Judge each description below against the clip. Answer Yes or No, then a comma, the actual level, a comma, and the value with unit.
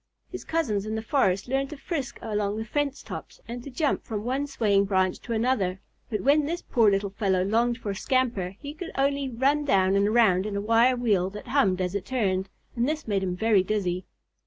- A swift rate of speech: Yes, fast, 220 wpm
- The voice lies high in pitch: Yes, high, 220 Hz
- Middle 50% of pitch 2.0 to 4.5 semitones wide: No, average, 5.1 semitones